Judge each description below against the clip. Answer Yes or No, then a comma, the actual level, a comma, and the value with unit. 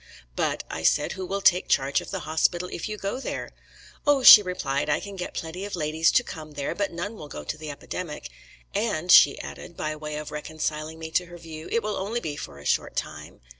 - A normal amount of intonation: Yes, average, 4.4 semitones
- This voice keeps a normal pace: No, fast, 230 wpm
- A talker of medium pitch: Yes, medium, 165 Hz